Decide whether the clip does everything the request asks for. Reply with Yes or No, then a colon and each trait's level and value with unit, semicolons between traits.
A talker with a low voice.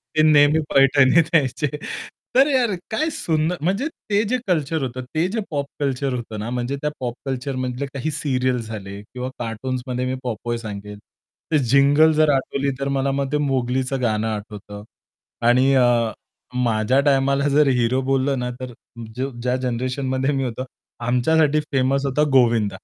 Yes: low, 130 Hz